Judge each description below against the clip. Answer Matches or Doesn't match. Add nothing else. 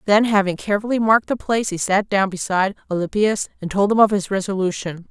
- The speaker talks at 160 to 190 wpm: Doesn't match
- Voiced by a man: Doesn't match